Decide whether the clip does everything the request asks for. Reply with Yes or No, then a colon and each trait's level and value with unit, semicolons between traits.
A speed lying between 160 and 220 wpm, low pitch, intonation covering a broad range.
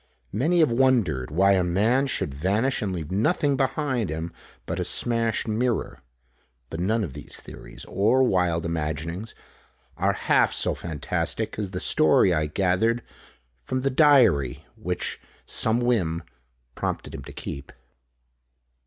No: average, 140 wpm; low, 100 Hz; wide, 6.8 semitones